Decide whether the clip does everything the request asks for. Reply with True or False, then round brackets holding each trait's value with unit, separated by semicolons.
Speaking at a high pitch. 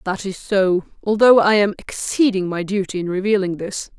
True (195 Hz)